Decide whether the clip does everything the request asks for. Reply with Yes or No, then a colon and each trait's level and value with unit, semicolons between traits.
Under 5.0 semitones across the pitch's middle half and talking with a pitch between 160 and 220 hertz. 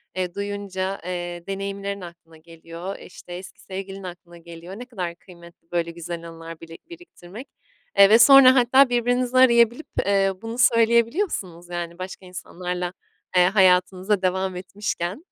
Yes: average, 4.2 semitones; high, 190 Hz